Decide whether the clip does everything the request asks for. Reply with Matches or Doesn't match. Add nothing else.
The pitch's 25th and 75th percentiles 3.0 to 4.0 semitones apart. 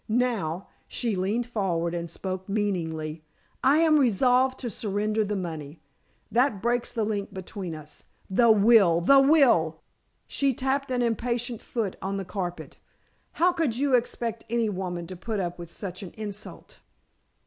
Doesn't match